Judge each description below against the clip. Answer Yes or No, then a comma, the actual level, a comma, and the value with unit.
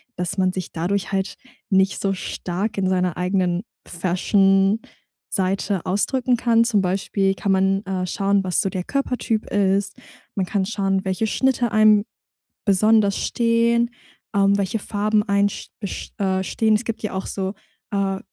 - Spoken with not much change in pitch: Yes, narrow, 2.1 semitones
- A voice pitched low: No, high, 195 Hz